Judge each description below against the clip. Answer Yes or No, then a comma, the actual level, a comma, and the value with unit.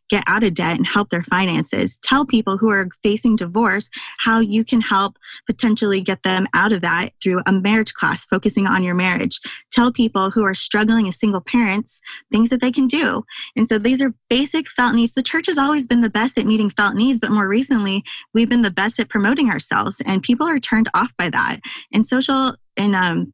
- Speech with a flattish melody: No, average, 4.0 semitones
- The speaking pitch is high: Yes, high, 220 Hz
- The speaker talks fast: Yes, fast, 215 wpm